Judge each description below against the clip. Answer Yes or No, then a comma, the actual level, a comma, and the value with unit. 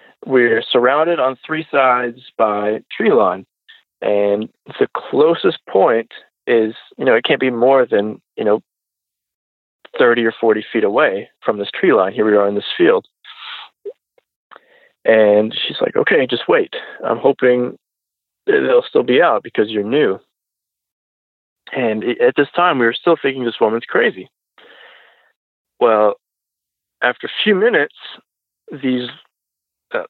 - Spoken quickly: No, average, 140 wpm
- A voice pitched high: No, low, 125 Hz